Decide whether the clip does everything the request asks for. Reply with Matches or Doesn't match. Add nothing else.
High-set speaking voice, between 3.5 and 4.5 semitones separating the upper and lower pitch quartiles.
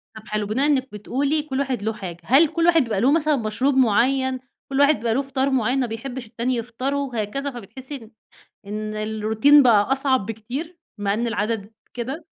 Matches